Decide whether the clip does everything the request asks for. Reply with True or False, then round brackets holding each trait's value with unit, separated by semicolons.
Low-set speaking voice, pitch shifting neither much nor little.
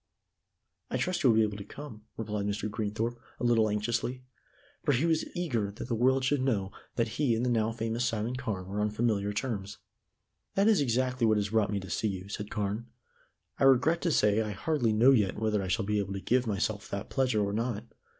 True (110 Hz; 3.5 semitones)